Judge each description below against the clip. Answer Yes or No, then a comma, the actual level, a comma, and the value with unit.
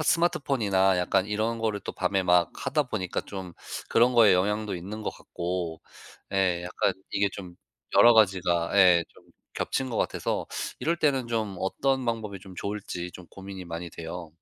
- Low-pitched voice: Yes, very low, 95 Hz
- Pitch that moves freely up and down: No, average, 3.8 semitones